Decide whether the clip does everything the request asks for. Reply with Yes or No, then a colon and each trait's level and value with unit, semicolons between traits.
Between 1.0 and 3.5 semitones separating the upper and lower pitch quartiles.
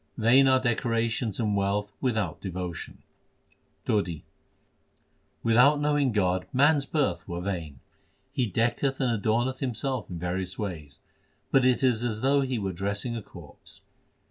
No: average, 5.3 semitones